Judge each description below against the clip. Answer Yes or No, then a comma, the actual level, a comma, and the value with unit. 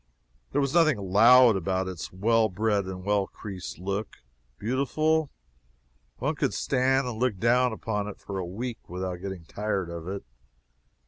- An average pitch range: Yes, average, 4.8 semitones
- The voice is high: No, low, 105 Hz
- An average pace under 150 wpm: No, average, 155 wpm